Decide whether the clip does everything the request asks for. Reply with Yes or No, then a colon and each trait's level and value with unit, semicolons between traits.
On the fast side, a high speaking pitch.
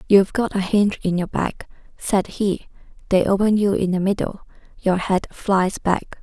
No: average, 185 wpm; high, 195 Hz